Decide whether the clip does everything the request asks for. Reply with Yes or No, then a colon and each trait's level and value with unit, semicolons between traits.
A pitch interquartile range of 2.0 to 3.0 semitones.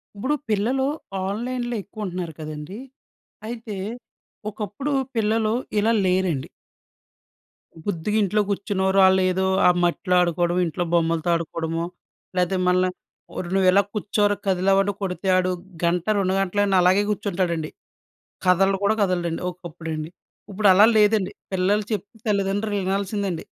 Yes: narrow, 2.5 semitones